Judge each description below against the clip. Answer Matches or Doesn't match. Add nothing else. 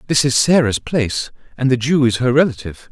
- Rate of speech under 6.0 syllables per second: Doesn't match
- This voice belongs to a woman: Doesn't match